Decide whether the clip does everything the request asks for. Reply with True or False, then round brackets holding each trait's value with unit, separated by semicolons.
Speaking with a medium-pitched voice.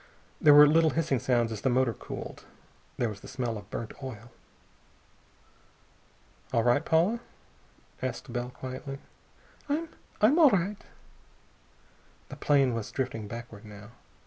False (130 Hz)